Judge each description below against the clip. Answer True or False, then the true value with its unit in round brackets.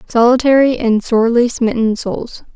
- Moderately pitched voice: False (235 Hz)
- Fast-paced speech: False (115 wpm)